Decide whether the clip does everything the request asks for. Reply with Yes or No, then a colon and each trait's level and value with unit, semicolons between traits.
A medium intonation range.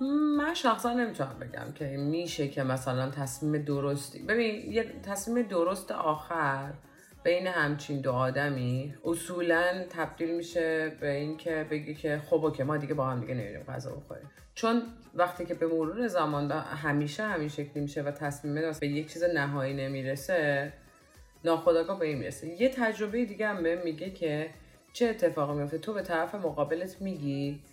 Yes: average, 3.6 semitones